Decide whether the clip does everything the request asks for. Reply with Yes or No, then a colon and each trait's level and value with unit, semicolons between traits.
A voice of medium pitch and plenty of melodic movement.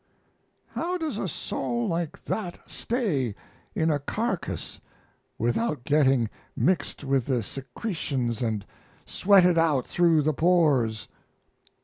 Yes: medium, 150 Hz; wide, 6.1 semitones